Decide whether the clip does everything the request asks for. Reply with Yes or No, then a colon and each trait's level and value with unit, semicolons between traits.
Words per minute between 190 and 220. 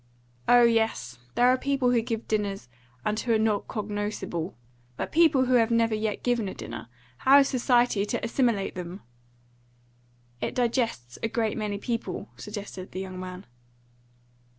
No: average, 155 wpm